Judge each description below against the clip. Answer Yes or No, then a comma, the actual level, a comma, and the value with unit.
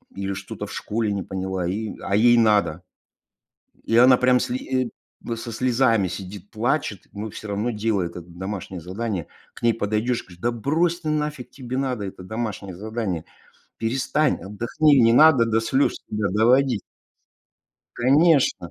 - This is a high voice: No, low, 115 Hz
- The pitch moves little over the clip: No, average, 4.2 semitones